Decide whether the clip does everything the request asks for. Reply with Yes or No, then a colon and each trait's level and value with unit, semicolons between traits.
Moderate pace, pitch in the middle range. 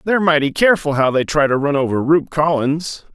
No: fast, 210 wpm; medium, 150 Hz